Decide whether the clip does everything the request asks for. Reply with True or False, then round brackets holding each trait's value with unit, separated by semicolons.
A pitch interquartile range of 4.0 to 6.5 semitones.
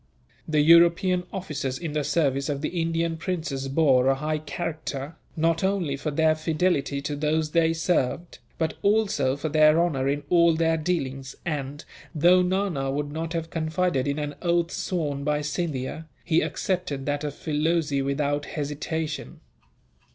False (2.8 semitones)